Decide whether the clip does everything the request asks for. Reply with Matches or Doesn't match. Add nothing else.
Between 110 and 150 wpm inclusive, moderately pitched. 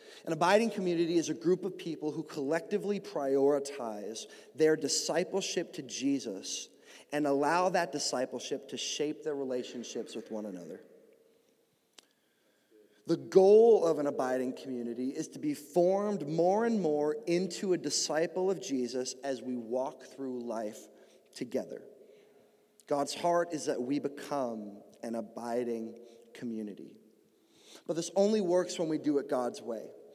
Matches